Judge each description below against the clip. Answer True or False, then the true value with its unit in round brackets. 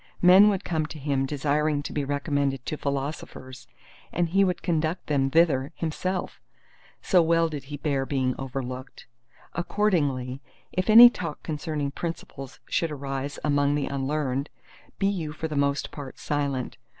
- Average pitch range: True (3.3 semitones)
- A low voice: False (145 Hz)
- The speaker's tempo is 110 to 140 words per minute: False (150 wpm)